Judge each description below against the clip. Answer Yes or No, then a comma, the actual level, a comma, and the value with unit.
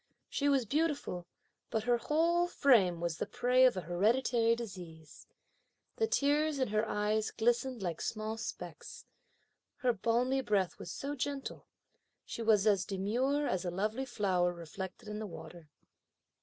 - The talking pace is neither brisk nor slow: Yes, average, 150 wpm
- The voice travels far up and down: Yes, wide, 5.7 semitones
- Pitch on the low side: No, high, 225 Hz